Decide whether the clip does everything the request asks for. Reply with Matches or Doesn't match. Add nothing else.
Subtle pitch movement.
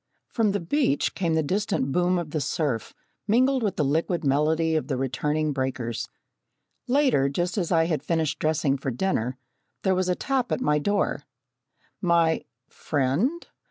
Doesn't match